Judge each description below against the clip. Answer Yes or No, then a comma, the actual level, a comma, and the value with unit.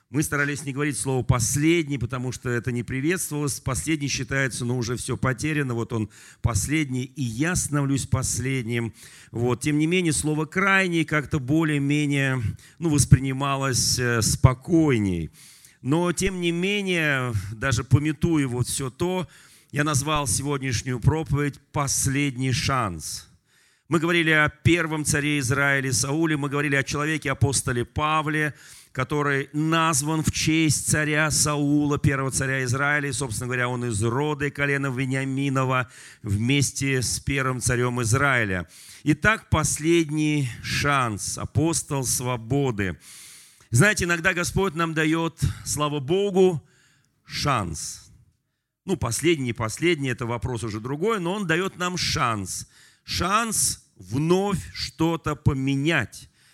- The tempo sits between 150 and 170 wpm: No, average, 120 wpm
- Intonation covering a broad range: No, average, 3.7 semitones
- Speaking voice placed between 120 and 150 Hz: Yes, medium, 140 Hz